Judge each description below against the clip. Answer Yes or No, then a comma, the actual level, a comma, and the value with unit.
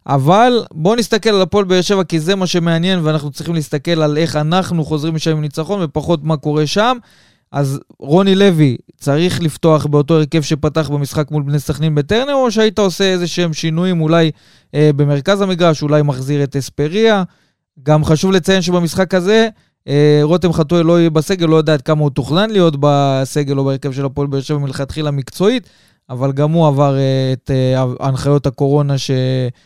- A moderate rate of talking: No, fast, 180 wpm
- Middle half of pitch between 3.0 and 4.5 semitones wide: Yes, average, 3.9 semitones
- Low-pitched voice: No, medium, 155 Hz